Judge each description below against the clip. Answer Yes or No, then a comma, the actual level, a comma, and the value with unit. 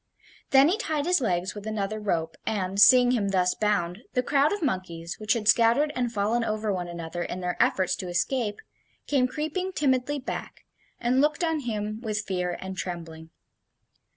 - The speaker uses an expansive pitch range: Yes, wide, 6.1 semitones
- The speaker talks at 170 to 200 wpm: Yes, average, 180 wpm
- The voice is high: Yes, high, 215 Hz